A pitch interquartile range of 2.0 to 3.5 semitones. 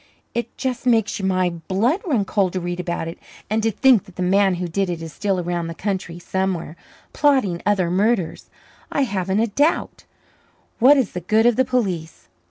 No: average, 4.7 semitones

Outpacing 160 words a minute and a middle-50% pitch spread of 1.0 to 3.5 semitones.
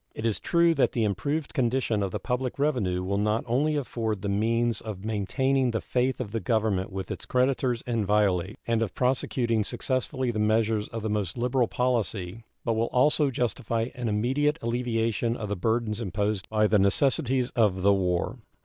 Yes: average, 180 wpm; average, 3.2 semitones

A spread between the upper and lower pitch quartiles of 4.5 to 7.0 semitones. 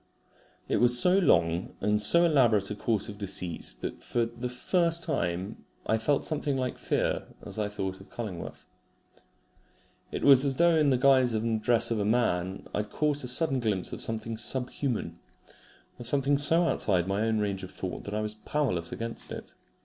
Yes: average, 5.1 semitones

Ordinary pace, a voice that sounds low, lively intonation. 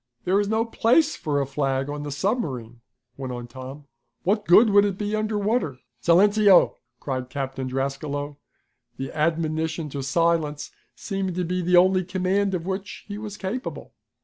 No: average, 160 wpm; medium, 170 Hz; wide, 6.3 semitones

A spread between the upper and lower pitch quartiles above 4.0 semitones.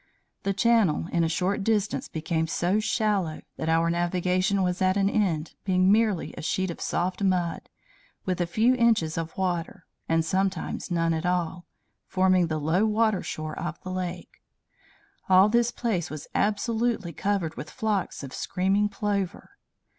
No: average, 3.3 semitones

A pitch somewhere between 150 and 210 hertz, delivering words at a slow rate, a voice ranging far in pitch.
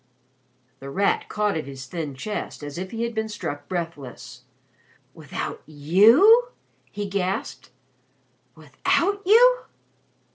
Yes: high, 190 Hz; slow, 115 wpm; wide, 7.6 semitones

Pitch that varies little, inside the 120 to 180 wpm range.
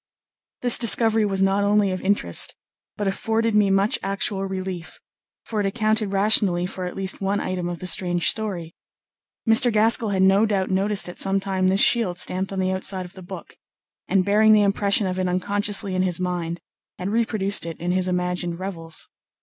No: narrow, 2.1 semitones; average, 190 wpm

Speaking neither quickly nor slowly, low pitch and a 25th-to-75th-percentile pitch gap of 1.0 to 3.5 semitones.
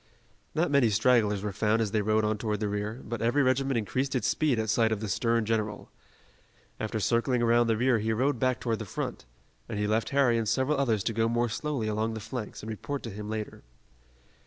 No: fast, 225 wpm; low, 115 Hz; average, 2.7 semitones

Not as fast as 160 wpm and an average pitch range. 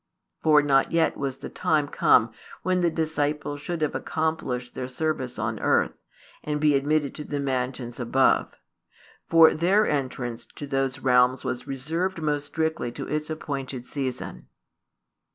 Yes: average, 150 wpm; average, 3.2 semitones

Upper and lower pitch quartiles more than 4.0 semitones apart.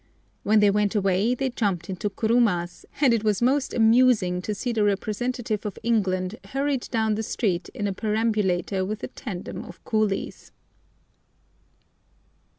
No: average, 3.2 semitones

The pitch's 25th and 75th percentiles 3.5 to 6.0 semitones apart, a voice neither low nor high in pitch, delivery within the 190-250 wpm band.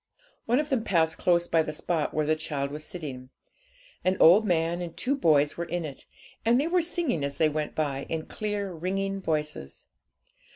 Yes: average, 4.4 semitones; medium, 165 Hz; average, 195 wpm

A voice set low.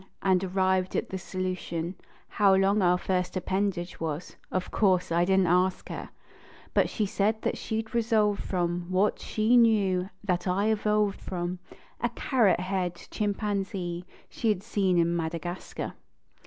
No: high, 190 Hz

